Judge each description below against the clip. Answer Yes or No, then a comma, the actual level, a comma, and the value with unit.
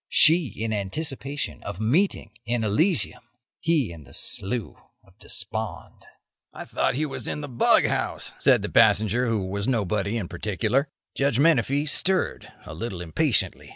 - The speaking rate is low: No, average, 155 wpm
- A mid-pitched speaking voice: No, low, 115 Hz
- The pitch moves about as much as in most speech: No, wide, 6.1 semitones